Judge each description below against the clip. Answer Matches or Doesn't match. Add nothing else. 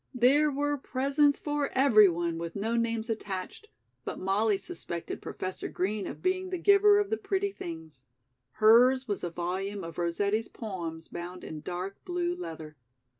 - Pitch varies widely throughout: Matches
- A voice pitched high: Matches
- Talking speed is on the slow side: Doesn't match